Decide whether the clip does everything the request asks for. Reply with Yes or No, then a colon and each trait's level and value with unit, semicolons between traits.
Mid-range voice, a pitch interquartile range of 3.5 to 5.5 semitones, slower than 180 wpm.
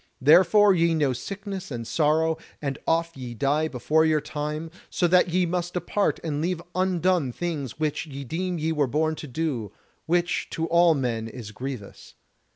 Yes: medium, 160 Hz; average, 3.9 semitones; average, 170 wpm